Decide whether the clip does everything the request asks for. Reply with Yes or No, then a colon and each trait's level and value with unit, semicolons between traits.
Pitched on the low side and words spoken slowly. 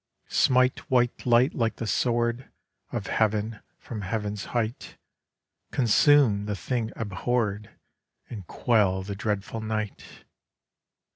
Yes: low, 110 Hz; slow, 110 wpm